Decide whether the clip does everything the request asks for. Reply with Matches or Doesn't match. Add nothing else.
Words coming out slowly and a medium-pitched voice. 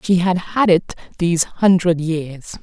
Doesn't match